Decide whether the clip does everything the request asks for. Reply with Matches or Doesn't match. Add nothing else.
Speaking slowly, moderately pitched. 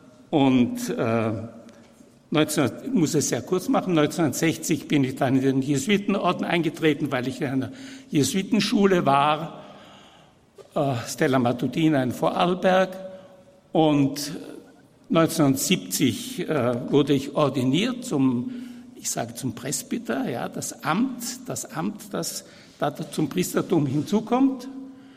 Matches